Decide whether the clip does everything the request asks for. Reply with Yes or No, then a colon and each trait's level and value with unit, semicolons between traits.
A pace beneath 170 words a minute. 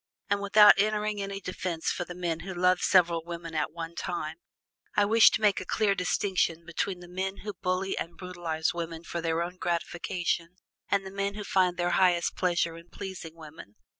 No: average, 195 wpm